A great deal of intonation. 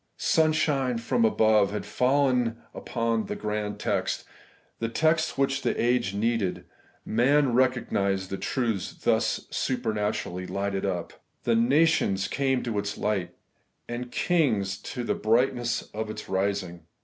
No: average, 4.1 semitones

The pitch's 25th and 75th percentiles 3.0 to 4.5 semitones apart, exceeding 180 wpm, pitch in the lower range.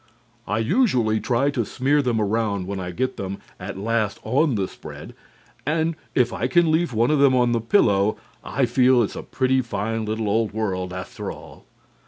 Yes: average, 4.1 semitones; average, 195 wpm; low, 115 Hz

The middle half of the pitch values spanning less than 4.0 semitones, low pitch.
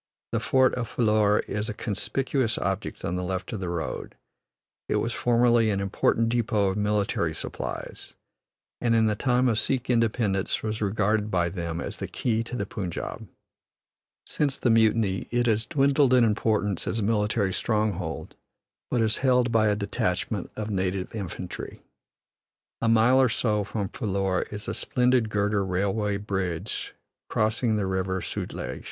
Yes: average, 3.0 semitones; low, 105 Hz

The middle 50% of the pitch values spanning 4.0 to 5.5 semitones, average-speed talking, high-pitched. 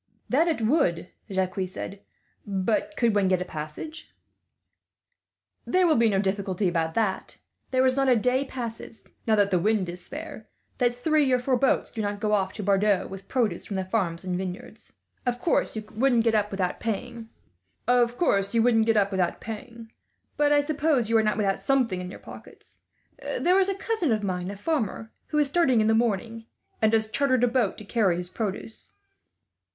Yes: average, 4.7 semitones; average, 180 wpm; high, 220 Hz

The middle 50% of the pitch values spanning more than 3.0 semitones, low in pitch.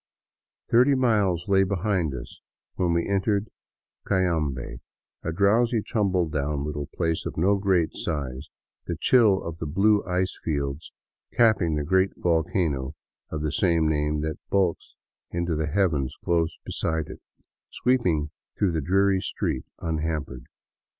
Yes: average, 4.3 semitones; very low, 85 Hz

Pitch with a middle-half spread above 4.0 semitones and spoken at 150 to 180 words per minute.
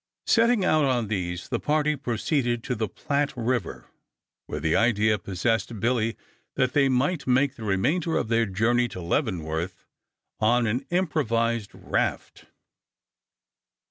No: average, 4.6 semitones; slow, 135 wpm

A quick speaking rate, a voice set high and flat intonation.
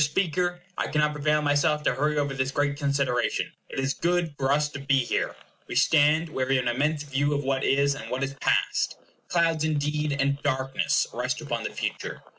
No: fast, 210 wpm; medium, 145 Hz; narrow, 1.8 semitones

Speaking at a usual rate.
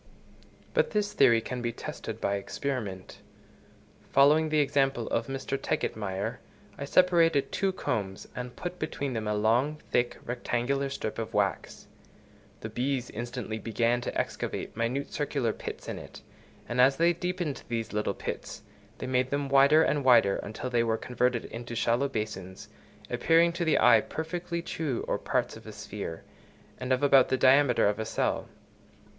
Yes: average, 160 wpm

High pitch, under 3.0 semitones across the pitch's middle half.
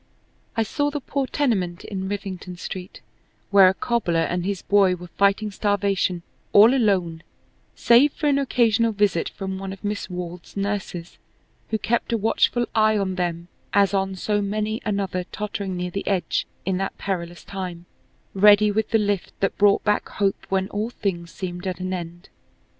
Yes: high, 195 Hz; narrow, 2.6 semitones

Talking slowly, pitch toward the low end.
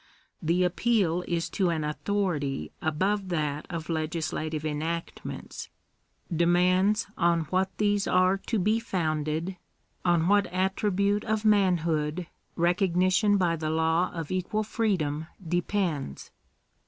No: slow, 125 wpm; medium, 175 Hz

